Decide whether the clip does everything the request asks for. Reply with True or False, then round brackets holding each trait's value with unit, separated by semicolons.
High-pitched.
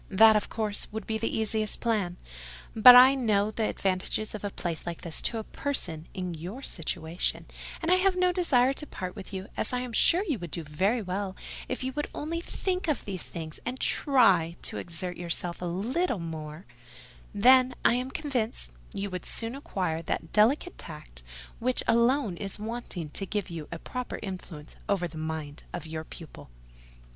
True (205 Hz)